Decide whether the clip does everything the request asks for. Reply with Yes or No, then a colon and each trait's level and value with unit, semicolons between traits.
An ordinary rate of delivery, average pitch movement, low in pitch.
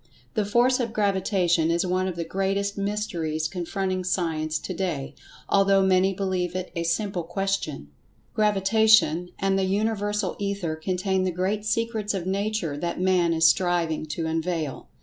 No: average, 155 wpm; average, 3.0 semitones; medium, 185 Hz